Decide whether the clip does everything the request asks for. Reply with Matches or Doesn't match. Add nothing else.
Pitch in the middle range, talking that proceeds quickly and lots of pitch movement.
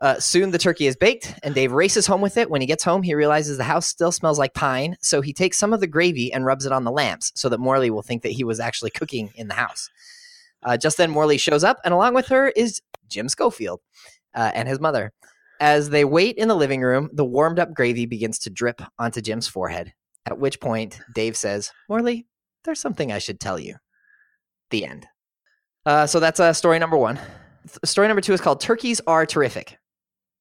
Matches